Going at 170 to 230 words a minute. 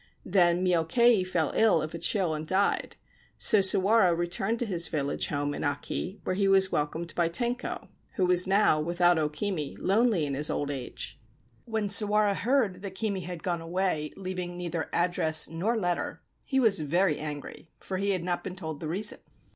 Yes: average, 185 wpm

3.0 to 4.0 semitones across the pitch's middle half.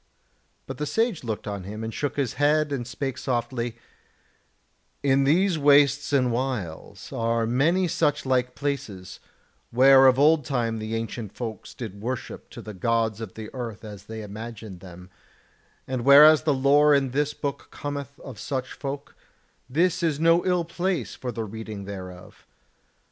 No: average, 4.4 semitones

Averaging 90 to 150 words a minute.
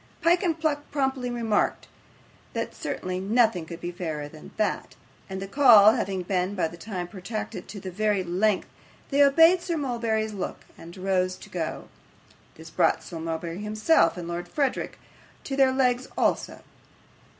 No: average, 165 wpm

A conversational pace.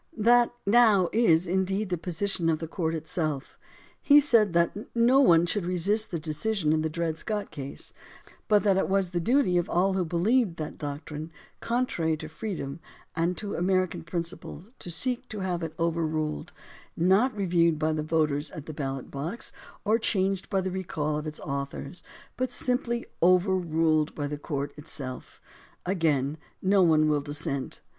Yes: average, 170 wpm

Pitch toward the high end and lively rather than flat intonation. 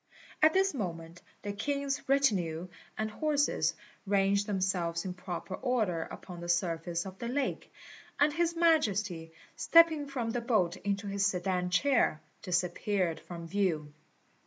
Yes: high, 200 Hz; wide, 7.1 semitones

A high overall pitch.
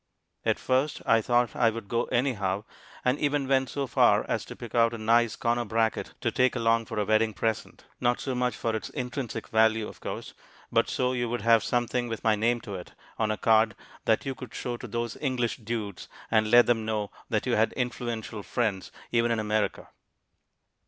No: low, 115 Hz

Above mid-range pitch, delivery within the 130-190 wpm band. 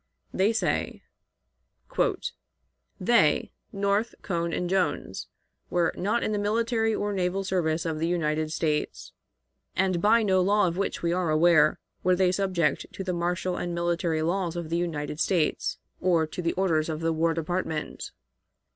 No: medium, 175 Hz; average, 155 wpm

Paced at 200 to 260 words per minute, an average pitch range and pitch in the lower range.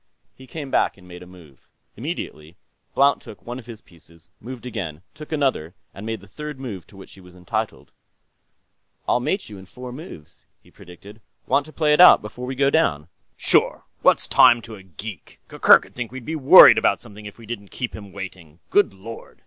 No: fast, 205 wpm; wide, 6.1 semitones; low, 110 Hz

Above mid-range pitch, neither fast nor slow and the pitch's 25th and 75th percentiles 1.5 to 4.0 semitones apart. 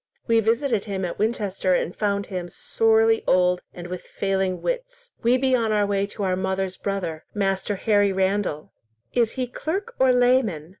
Yes: high, 205 Hz; average, 170 wpm; average, 3.7 semitones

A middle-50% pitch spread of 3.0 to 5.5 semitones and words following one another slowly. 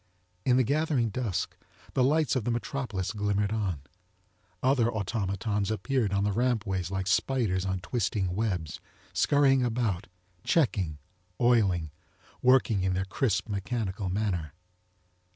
Yes: average, 4.6 semitones; slow, 125 wpm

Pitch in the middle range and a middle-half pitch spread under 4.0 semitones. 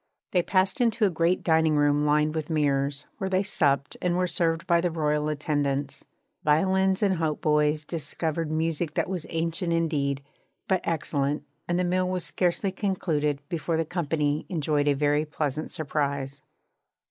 Yes: medium, 160 Hz; average, 3.1 semitones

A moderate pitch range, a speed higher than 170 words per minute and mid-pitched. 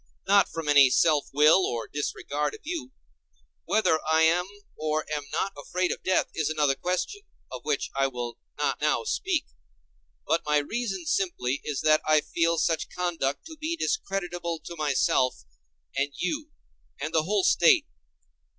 No: average, 4.2 semitones; average, 160 wpm; medium, 160 Hz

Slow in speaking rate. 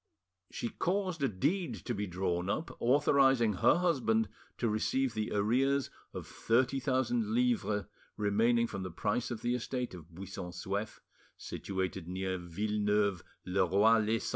No: average, 150 wpm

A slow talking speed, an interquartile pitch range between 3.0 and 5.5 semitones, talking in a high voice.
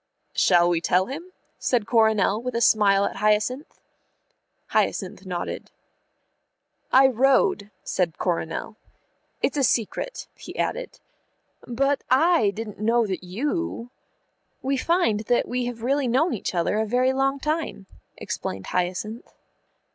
Yes: slow, 130 wpm; average, 5.2 semitones; high, 230 Hz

